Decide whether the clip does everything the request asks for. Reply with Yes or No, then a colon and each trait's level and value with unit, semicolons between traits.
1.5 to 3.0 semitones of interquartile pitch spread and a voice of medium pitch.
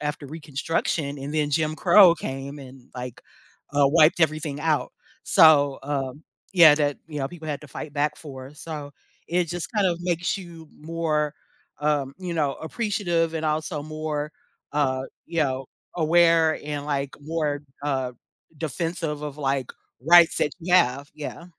Yes: narrow, 2.5 semitones; medium, 150 Hz